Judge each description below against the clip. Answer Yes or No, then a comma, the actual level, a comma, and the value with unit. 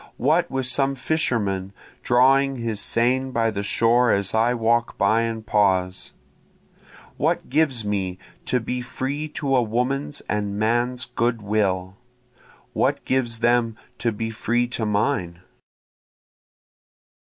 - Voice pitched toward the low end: Yes, low, 115 Hz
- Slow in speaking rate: Yes, slow, 130 wpm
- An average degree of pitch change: Yes, average, 3.4 semitones